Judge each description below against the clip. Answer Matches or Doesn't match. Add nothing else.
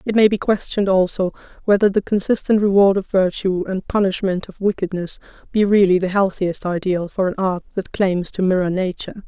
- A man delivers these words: Doesn't match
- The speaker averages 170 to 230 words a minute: Matches